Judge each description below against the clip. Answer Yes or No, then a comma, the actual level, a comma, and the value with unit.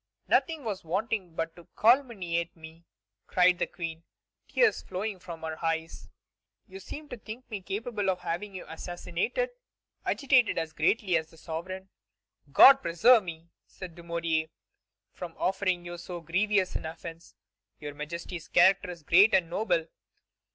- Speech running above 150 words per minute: No, average, 145 wpm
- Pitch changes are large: No, average, 3.7 semitones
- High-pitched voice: No, medium, 180 Hz